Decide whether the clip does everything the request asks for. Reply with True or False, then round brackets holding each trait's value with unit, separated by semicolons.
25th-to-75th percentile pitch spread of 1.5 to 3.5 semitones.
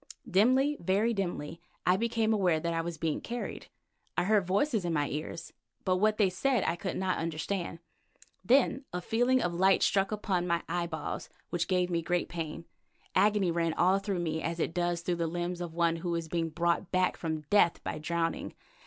True (3.0 semitones)